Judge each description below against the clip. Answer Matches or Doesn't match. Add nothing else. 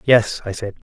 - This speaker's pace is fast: Doesn't match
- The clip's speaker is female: Doesn't match